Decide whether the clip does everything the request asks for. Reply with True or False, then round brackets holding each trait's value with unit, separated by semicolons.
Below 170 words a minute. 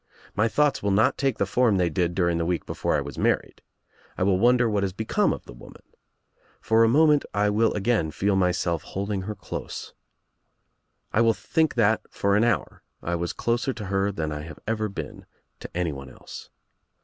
False (200 wpm)